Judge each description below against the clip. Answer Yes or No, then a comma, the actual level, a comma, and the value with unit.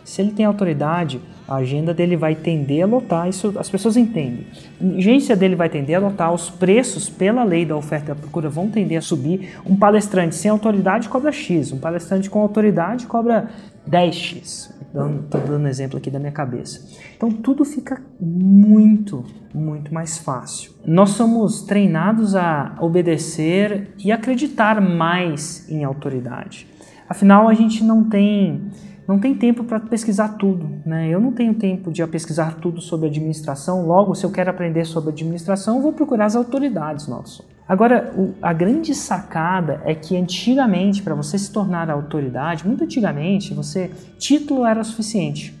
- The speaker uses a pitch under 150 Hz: No, medium, 185 Hz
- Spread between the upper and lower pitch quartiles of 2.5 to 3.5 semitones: No, average, 4.7 semitones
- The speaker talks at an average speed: Yes, average, 165 wpm